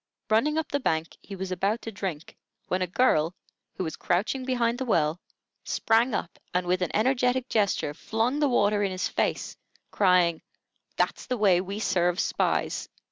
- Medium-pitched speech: No, high, 200 Hz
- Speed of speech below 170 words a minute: No, average, 175 wpm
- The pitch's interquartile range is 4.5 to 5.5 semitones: Yes, average, 5.2 semitones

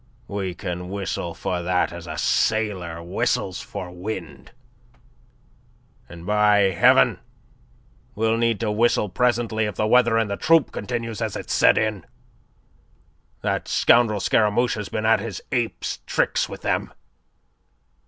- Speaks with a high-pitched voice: No, low, 105 Hz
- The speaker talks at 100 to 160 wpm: Yes, slow, 135 wpm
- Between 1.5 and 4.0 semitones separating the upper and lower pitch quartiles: Yes, average, 3.6 semitones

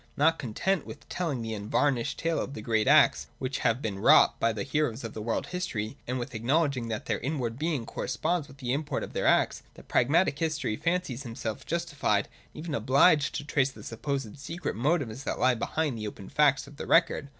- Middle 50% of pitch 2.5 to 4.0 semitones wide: No, average, 5.1 semitones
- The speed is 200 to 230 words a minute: Yes, fast, 205 wpm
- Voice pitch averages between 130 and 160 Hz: Yes, low, 135 Hz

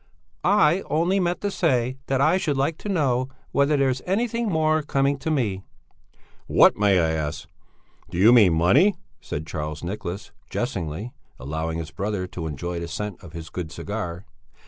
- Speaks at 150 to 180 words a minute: Yes, average, 170 wpm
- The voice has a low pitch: Yes, low, 110 Hz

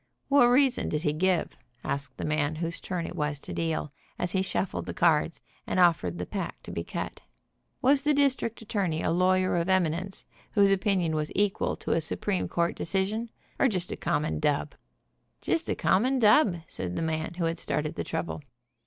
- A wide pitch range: No, average, 4.2 semitones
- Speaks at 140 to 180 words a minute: No, average, 195 wpm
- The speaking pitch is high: No, medium, 175 Hz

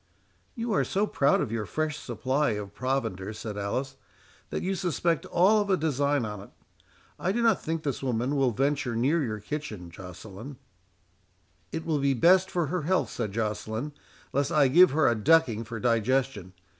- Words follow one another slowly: No, average, 175 wpm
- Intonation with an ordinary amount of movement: No, wide, 6.4 semitones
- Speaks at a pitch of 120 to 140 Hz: Yes, low, 135 Hz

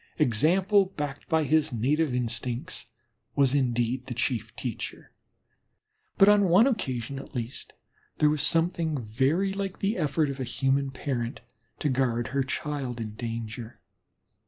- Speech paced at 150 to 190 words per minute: No, average, 140 wpm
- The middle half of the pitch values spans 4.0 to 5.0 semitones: Yes, average, 4.7 semitones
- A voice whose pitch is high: No, low, 135 Hz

